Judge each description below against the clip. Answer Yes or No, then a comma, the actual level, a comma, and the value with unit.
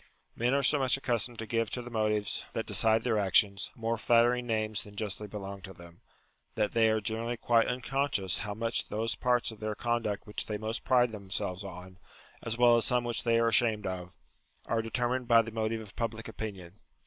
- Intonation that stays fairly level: Yes, narrow, 2.3 semitones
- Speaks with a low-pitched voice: Yes, low, 110 Hz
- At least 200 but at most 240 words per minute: Yes, fast, 205 wpm